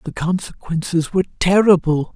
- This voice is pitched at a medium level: Yes, medium, 175 Hz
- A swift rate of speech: No, slow, 110 wpm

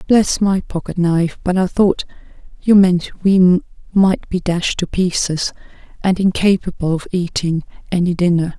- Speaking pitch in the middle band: Yes, medium, 180 Hz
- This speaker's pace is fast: No, average, 145 wpm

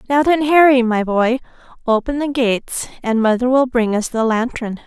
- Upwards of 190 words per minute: No, average, 185 wpm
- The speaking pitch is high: Yes, high, 245 Hz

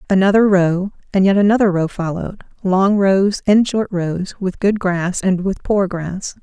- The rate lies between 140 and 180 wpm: Yes, average, 170 wpm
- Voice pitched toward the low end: No, high, 190 Hz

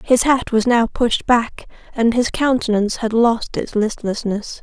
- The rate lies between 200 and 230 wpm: No, average, 170 wpm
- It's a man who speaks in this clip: No, female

